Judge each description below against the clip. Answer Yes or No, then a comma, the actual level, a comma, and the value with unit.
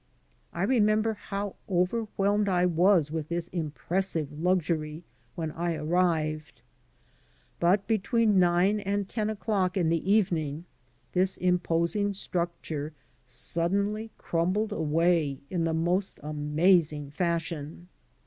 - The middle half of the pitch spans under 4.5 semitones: Yes, average, 3.6 semitones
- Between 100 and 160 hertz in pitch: No, medium, 175 Hz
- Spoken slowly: Yes, slow, 110 wpm